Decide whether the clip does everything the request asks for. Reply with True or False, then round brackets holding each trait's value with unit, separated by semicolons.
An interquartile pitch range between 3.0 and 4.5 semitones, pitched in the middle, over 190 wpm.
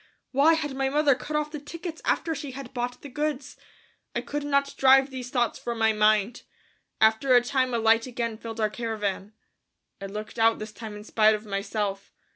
False (4.2 semitones; 240 Hz; 200 wpm)